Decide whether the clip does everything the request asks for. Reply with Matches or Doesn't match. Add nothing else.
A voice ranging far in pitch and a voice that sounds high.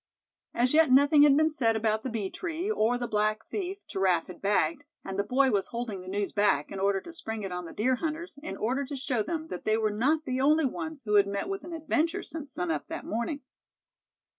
Matches